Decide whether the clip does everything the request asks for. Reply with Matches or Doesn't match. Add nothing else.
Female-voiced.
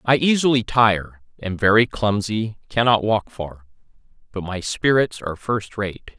Doesn't match